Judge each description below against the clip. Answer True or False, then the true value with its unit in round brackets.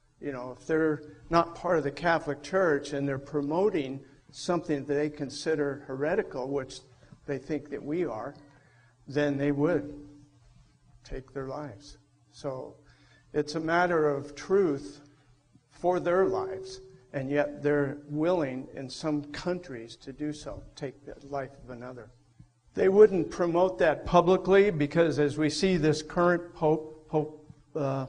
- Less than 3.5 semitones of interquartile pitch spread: True (2.8 semitones)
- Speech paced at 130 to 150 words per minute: True (145 wpm)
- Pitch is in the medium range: True (145 Hz)